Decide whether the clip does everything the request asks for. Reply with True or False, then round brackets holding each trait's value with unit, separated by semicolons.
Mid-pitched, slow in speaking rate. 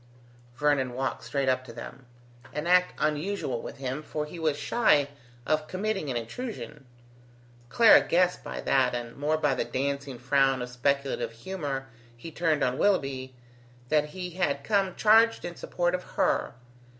False (145 Hz; 160 wpm)